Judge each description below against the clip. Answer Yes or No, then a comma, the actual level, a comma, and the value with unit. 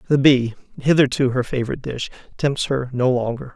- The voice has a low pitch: Yes, low, 130 Hz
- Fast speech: No, average, 170 wpm